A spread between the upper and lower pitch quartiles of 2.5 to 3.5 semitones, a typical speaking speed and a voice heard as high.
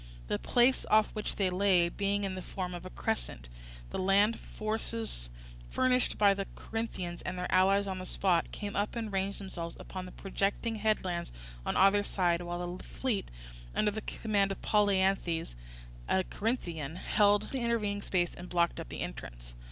Yes: average, 2.9 semitones; average, 175 wpm; high, 195 Hz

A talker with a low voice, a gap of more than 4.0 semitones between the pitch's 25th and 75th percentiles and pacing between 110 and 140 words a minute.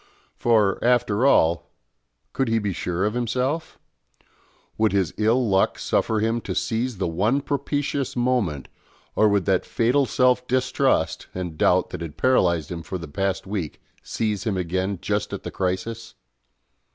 No: low, 110 Hz; average, 5.2 semitones; average, 155 wpm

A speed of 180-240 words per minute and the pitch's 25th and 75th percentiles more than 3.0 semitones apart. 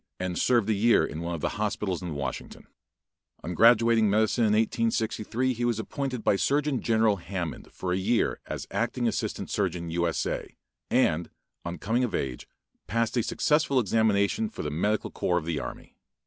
Yes: average, 185 wpm; average, 4.8 semitones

